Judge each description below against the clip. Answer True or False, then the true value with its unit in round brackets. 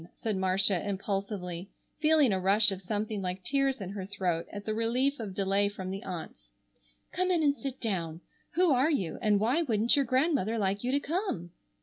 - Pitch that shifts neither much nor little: False (5.8 semitones)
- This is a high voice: True (205 Hz)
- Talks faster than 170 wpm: True (195 wpm)